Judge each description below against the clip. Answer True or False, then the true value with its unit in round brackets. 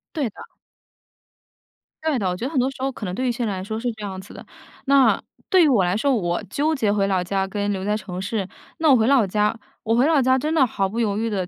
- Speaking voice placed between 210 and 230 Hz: True (220 Hz)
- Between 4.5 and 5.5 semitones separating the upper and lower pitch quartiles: True (5.2 semitones)